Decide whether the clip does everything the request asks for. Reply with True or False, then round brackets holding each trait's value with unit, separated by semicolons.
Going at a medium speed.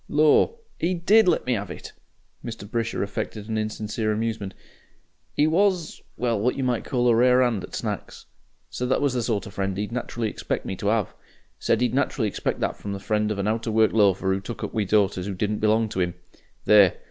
False (220 wpm)